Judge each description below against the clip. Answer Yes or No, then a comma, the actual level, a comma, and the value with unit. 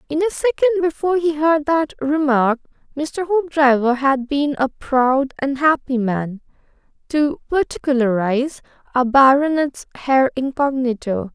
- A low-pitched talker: No, very high, 280 Hz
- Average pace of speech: No, slow, 120 wpm